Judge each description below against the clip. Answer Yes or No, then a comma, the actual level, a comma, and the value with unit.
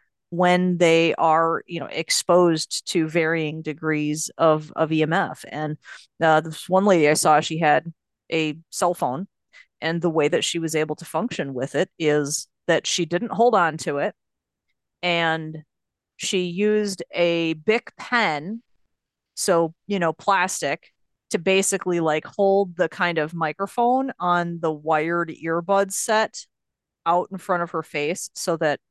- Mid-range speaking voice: Yes, medium, 165 Hz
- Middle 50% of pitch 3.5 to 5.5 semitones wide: No, average, 2.9 semitones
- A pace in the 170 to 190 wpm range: No, average, 155 wpm